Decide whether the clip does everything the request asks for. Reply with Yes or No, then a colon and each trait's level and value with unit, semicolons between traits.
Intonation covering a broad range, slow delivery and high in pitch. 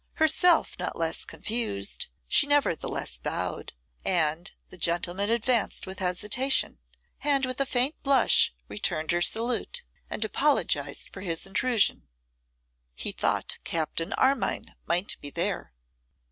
Yes: wide, 7.6 semitones; slow, 120 wpm; high, 210 Hz